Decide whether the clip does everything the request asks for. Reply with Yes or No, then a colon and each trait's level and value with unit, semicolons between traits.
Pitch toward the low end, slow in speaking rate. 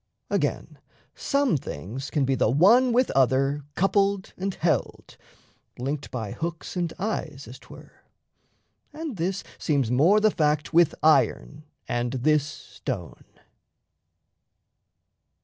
No: medium, 155 Hz; slow, 115 wpm